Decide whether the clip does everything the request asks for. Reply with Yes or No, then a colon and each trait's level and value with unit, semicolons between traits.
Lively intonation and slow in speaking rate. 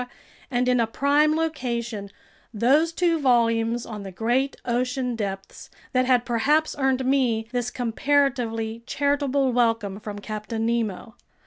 No: average, 3.2 semitones; slow, 130 wpm